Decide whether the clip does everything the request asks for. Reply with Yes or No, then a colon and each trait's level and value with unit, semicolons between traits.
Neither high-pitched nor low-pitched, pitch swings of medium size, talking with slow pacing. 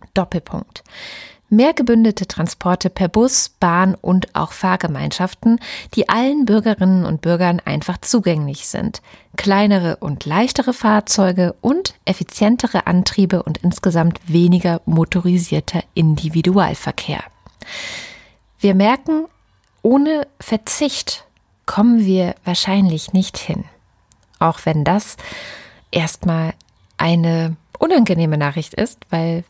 Yes: medium, 180 Hz; average, 4.4 semitones; slow, 100 wpm